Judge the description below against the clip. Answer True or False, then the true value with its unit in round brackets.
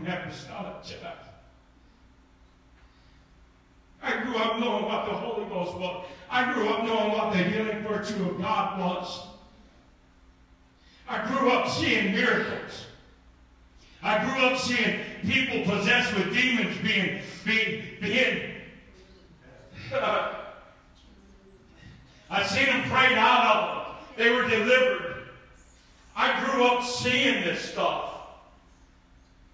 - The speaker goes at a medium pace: False (110 wpm)